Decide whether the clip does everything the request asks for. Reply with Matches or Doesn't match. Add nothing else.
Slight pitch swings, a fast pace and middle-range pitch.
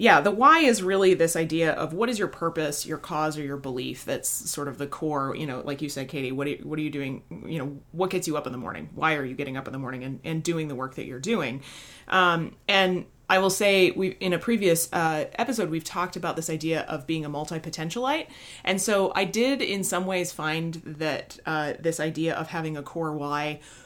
Doesn't match